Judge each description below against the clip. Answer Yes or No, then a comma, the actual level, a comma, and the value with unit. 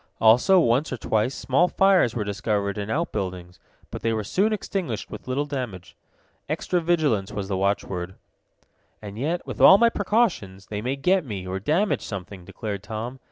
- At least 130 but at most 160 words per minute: No, average, 170 wpm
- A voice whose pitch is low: Yes, low, 115 Hz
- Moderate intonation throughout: No, wide, 8.6 semitones